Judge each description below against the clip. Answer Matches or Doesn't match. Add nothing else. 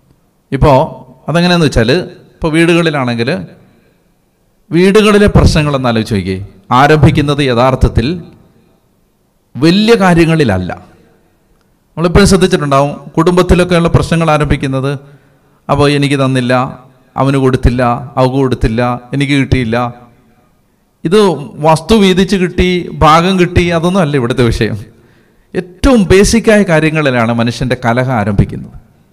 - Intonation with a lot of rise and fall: Matches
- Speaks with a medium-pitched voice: Matches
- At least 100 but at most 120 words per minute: Doesn't match